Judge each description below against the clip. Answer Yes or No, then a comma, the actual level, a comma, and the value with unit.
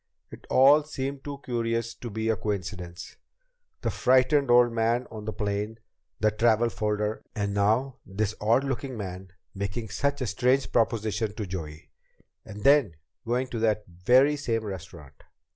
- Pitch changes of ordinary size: Yes, average, 3.6 semitones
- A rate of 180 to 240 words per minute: No, average, 155 wpm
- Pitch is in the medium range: No, low, 110 Hz